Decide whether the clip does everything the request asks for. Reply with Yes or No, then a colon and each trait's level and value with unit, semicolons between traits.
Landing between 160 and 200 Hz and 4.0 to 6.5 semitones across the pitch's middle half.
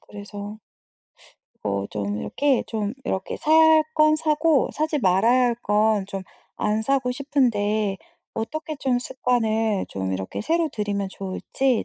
No: high, 220 Hz; wide, 5.6 semitones